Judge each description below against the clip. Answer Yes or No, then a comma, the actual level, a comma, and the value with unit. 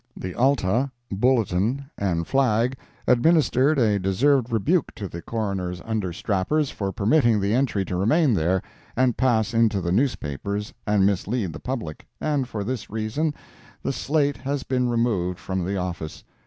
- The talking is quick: No, average, 150 wpm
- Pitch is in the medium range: No, low, 110 Hz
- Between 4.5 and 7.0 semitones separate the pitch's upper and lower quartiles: Yes, wide, 5.4 semitones